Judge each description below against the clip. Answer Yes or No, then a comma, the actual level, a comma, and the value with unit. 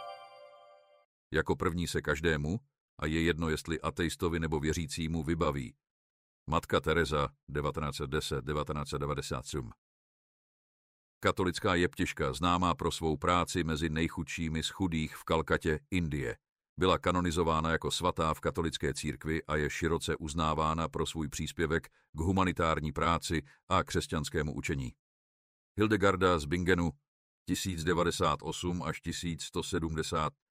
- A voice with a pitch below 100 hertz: Yes, very low, 80 Hz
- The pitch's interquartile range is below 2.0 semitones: No, narrow, 2.4 semitones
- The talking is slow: Yes, slow, 105 wpm